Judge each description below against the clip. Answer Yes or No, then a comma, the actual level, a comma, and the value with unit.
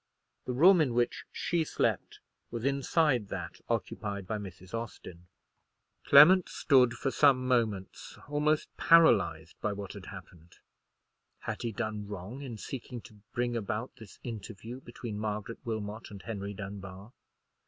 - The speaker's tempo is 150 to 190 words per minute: No, average, 140 wpm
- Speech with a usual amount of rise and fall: Yes, average, 4.1 semitones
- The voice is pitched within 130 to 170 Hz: No, low, 115 Hz